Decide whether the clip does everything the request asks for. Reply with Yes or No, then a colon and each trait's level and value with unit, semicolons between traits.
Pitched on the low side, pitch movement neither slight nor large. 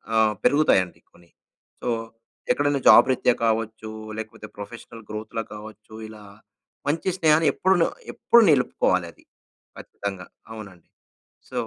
Yes: low, 110 Hz; average, 4.6 semitones